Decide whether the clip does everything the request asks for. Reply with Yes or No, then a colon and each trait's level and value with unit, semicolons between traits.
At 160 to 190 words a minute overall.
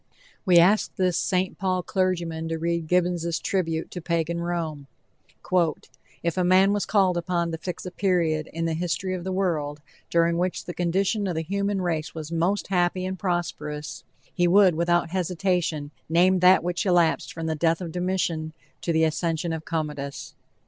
Yes: average, 175 wpm